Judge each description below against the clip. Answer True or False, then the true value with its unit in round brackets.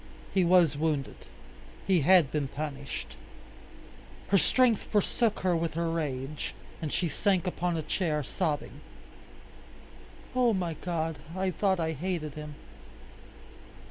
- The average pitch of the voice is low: False (165 Hz)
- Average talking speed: False (125 wpm)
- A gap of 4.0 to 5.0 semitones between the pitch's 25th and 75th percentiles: False (3.6 semitones)